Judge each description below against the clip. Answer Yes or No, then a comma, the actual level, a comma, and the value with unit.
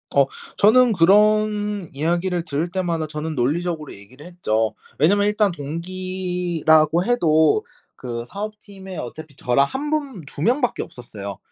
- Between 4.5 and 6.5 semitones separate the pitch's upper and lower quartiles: Yes, average, 5.3 semitones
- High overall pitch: No, medium, 175 Hz